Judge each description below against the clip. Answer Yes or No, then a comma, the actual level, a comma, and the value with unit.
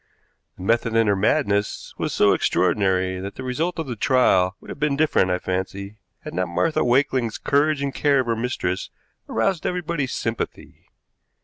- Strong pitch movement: Yes, wide, 6.4 semitones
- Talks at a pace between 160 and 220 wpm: Yes, average, 175 wpm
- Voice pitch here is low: Yes, low, 115 Hz